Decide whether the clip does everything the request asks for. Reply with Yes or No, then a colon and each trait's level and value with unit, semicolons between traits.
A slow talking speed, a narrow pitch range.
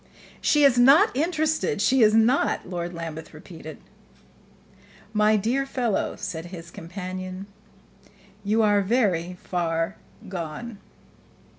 No: slow, 110 wpm; wide, 5.6 semitones